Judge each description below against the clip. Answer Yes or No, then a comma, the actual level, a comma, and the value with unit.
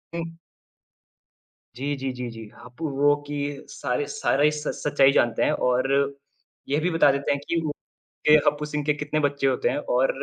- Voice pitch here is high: No, medium, 145 Hz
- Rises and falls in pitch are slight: Yes, narrow, 2.1 semitones